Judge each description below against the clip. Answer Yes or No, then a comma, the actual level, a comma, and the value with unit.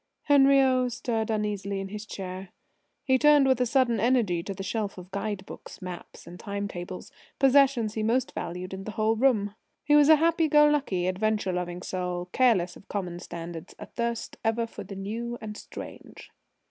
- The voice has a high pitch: Yes, high, 215 Hz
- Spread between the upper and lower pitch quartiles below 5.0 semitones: No, average, 5.3 semitones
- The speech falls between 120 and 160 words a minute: No, average, 175 wpm